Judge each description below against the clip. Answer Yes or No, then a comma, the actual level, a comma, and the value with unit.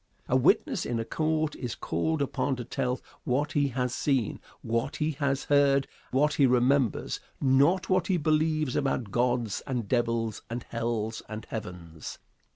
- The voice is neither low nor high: No, low, 130 Hz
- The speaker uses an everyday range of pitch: Yes, average, 3.9 semitones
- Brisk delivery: No, average, 160 wpm